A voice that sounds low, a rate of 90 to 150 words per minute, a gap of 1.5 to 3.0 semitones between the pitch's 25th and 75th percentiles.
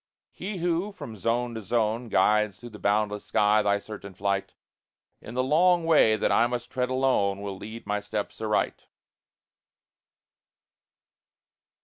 No: low, 110 Hz; average, 140 wpm; average, 3.7 semitones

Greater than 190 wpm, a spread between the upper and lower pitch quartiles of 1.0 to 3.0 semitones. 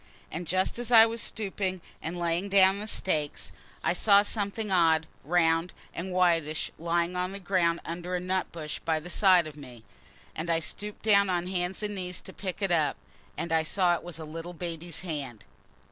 Yes: average, 200 wpm; narrow, 2.6 semitones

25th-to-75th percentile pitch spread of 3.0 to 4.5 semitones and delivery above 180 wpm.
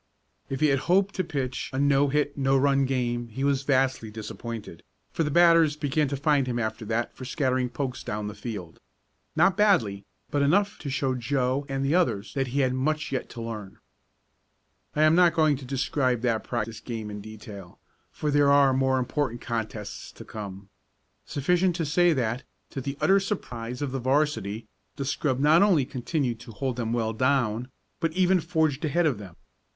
Yes: average, 4.2 semitones; average, 190 wpm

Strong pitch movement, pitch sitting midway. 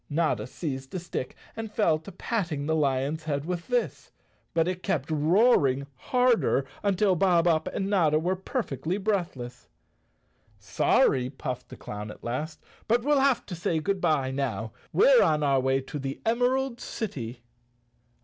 Yes: wide, 6.7 semitones; medium, 160 Hz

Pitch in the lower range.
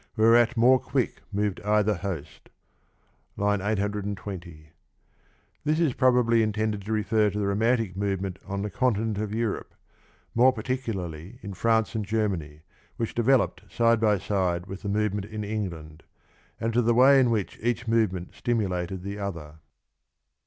Yes: low, 105 Hz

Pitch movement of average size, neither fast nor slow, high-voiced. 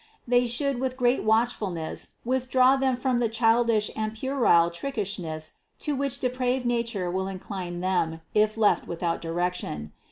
No: wide, 5.8 semitones; average, 155 wpm; high, 225 Hz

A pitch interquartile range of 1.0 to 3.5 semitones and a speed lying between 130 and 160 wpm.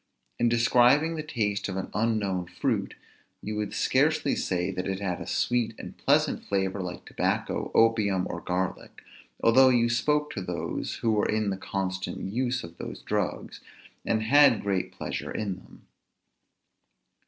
No: average, 3.9 semitones; average, 155 wpm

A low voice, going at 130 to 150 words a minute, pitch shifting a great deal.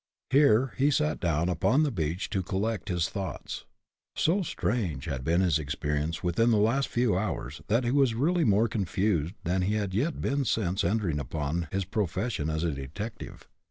No: very low, 95 Hz; average, 180 wpm; wide, 6.0 semitones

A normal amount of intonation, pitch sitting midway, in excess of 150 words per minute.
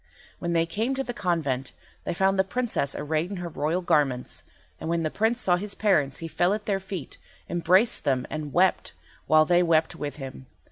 Yes: average, 4.0 semitones; medium, 170 Hz; average, 200 wpm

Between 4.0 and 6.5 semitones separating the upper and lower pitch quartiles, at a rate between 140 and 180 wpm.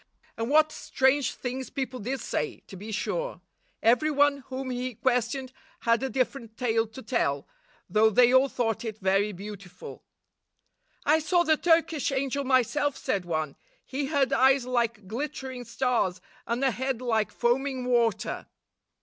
No: average, 3.4 semitones; average, 150 wpm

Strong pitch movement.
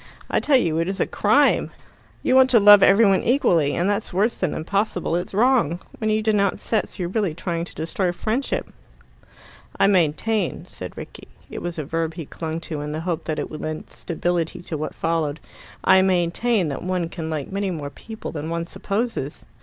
No: average, 4.2 semitones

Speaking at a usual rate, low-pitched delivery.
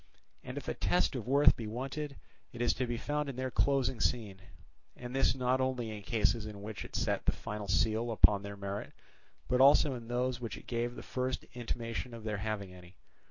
No: fast, 215 wpm; low, 120 Hz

